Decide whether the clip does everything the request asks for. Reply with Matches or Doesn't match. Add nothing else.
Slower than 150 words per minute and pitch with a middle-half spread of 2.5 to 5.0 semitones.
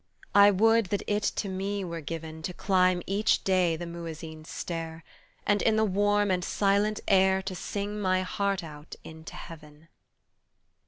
Doesn't match